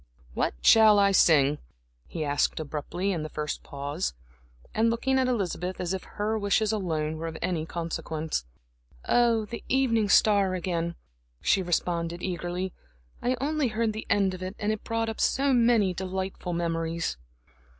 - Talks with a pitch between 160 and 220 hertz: Yes, medium, 185 Hz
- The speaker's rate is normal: Yes, average, 160 wpm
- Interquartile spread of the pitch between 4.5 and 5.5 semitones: Yes, average, 4.8 semitones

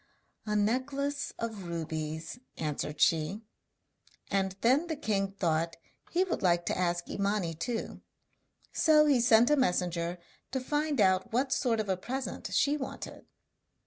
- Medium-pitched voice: No, high, 210 Hz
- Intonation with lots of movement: Yes, wide, 7.2 semitones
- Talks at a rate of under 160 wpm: Yes, average, 145 wpm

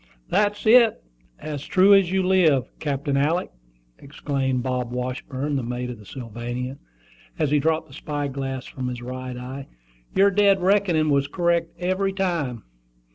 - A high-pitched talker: No, medium, 145 Hz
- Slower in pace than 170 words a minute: Yes, average, 155 wpm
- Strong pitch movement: Yes, wide, 6.0 semitones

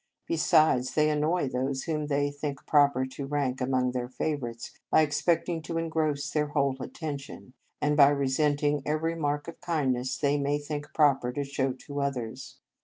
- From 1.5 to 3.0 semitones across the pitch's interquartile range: Yes, narrow, 2.4 semitones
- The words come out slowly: No, average, 175 wpm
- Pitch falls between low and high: Yes, medium, 145 Hz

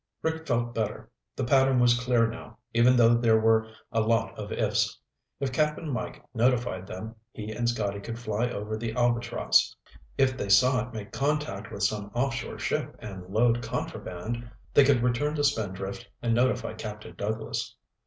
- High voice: No, low, 115 Hz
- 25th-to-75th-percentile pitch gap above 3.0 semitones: No, narrow, 2.6 semitones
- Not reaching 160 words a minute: No, average, 170 wpm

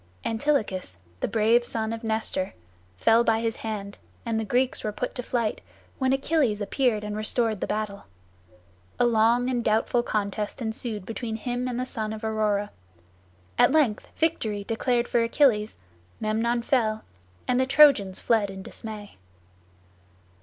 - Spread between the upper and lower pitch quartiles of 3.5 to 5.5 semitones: No, narrow, 2.4 semitones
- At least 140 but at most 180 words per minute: Yes, average, 150 wpm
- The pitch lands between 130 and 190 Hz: No, high, 225 Hz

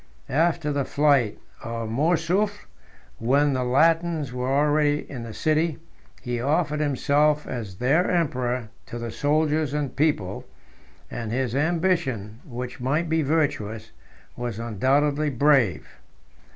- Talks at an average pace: No, slow, 125 wpm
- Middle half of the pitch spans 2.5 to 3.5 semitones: No, average, 4.1 semitones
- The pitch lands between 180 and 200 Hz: No, medium, 140 Hz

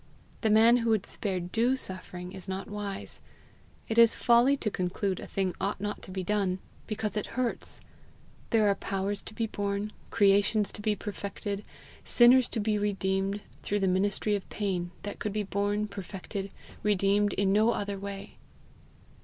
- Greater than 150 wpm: Yes, average, 170 wpm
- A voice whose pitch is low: No, high, 205 Hz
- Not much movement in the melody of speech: Yes, narrow, 1.7 semitones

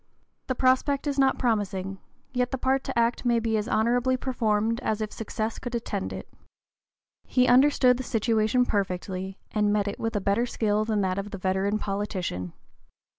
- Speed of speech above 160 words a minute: Yes, average, 175 wpm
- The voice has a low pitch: No, high, 220 Hz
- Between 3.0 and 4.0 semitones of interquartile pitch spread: Yes, average, 3.6 semitones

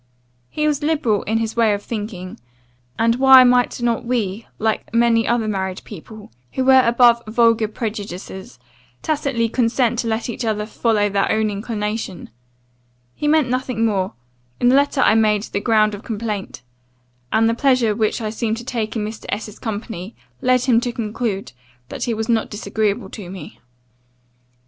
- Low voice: No, high, 225 Hz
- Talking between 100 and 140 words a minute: No, average, 170 wpm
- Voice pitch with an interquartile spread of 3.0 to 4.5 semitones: No, narrow, 2.4 semitones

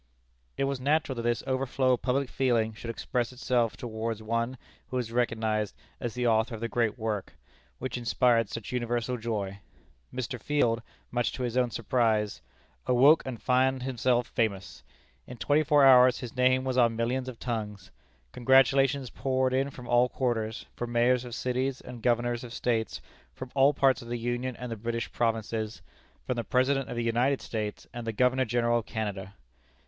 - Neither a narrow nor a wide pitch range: No, narrow, 2.0 semitones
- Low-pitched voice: Yes, low, 120 Hz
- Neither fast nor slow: Yes, average, 180 wpm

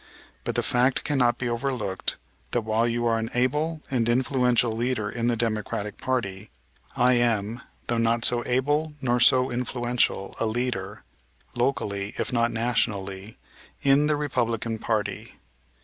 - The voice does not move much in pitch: Yes, narrow, 2.2 semitones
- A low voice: Yes, low, 120 Hz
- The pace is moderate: Yes, average, 145 wpm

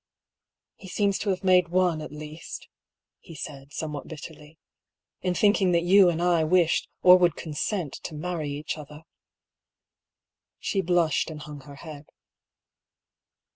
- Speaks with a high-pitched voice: No, medium, 165 Hz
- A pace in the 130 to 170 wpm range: Yes, average, 165 wpm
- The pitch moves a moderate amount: Yes, average, 3.2 semitones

